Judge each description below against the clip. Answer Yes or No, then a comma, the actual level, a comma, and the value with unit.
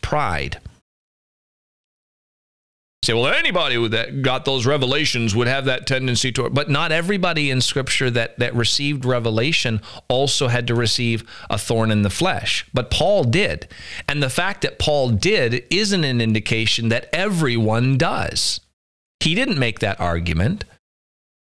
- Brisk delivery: No, average, 150 wpm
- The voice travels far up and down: No, average, 3.8 semitones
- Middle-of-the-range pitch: No, low, 125 Hz